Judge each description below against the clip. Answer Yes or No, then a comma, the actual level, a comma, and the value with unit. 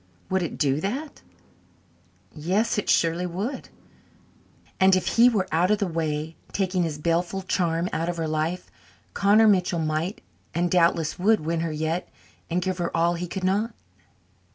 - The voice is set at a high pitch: No, medium, 175 Hz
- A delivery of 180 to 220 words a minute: No, average, 165 wpm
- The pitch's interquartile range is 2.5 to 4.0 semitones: Yes, average, 2.8 semitones